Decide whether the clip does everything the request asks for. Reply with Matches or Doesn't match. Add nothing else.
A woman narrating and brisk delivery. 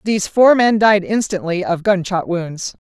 Doesn't match